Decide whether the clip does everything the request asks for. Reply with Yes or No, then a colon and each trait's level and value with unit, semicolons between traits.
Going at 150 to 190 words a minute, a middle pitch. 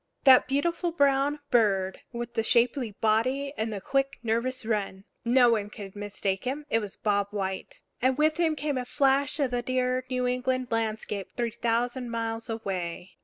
No: average, 170 wpm; high, 240 Hz